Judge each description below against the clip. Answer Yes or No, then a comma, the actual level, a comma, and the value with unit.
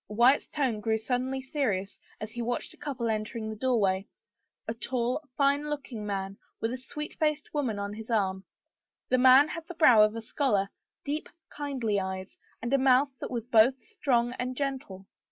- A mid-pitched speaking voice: No, high, 245 Hz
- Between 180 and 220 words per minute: Yes, average, 185 wpm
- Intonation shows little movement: No, average, 4.3 semitones